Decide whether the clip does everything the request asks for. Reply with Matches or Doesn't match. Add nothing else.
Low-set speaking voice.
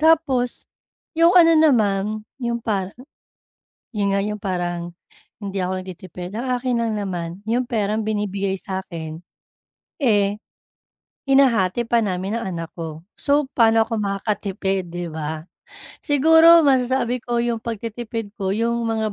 Doesn't match